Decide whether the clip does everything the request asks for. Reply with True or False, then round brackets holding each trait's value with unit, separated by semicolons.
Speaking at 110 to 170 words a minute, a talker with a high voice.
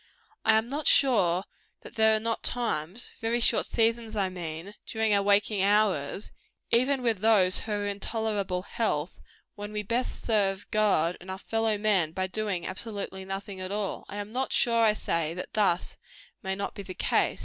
False (185 wpm; 205 Hz)